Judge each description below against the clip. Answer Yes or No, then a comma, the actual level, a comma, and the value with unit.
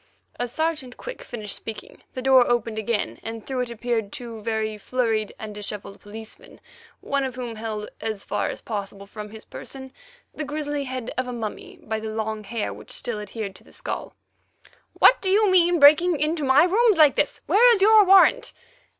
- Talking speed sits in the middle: Yes, average, 190 wpm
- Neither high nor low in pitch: No, high, 240 Hz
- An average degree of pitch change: No, wide, 5.9 semitones